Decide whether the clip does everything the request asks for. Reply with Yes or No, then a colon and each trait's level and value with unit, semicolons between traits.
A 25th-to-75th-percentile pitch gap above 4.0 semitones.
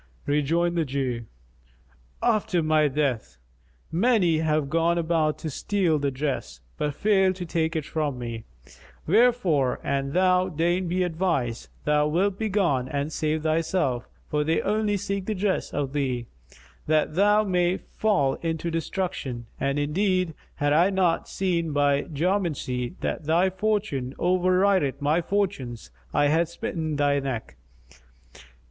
Yes: average, 4.5 semitones